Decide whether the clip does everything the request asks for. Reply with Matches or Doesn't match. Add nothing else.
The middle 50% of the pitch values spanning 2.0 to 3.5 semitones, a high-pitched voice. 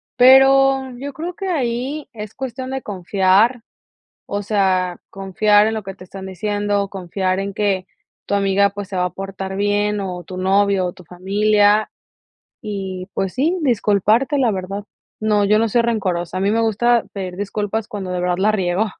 Matches